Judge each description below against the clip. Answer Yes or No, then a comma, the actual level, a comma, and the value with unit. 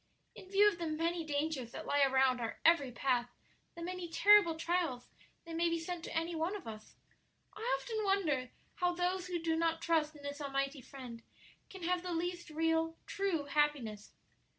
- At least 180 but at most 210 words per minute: Yes, average, 185 wpm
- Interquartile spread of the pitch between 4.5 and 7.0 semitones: No, average, 3.9 semitones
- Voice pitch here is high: Yes, very high, 325 Hz